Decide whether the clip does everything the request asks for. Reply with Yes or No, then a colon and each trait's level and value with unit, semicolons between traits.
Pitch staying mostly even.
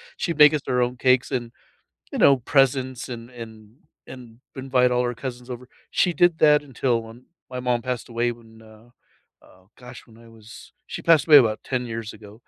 Yes: narrow, 2.3 semitones